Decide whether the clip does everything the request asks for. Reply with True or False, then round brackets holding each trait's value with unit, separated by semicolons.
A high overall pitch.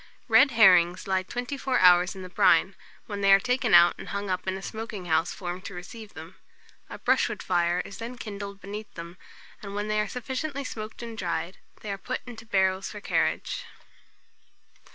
True (200 Hz)